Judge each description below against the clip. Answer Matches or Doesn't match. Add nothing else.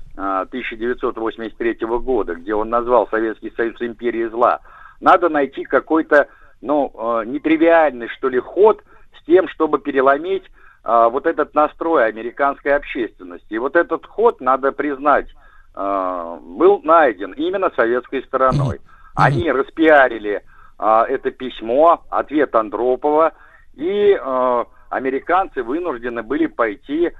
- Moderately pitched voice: Matches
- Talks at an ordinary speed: Doesn't match